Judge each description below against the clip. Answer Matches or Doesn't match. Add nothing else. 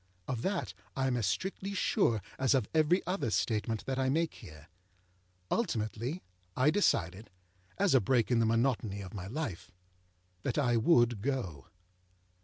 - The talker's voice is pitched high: Doesn't match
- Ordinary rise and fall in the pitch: Doesn't match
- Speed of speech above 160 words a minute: Doesn't match